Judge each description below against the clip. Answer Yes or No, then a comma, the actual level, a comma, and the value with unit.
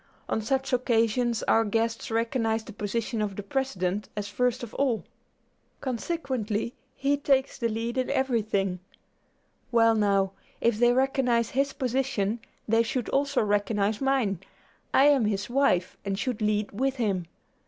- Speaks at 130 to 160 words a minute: Yes, average, 145 wpm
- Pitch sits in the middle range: No, high, 230 Hz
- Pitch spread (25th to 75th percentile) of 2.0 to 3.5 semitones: No, average, 3.9 semitones